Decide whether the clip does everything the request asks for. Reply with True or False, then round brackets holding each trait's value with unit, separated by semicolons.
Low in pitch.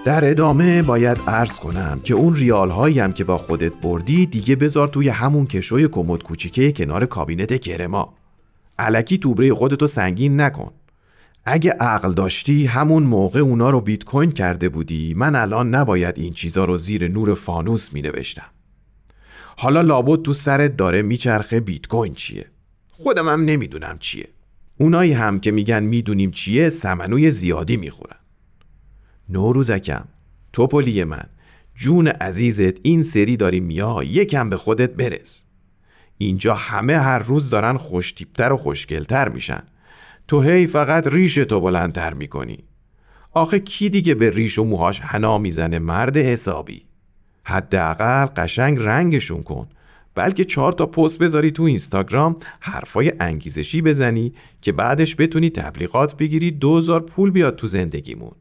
True (120 Hz)